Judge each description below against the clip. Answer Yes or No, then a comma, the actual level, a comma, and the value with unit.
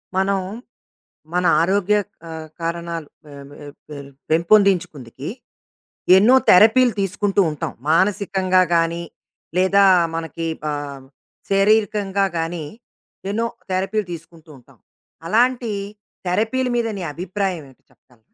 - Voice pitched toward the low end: No, medium, 185 Hz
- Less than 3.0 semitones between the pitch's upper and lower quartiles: No, average, 3.8 semitones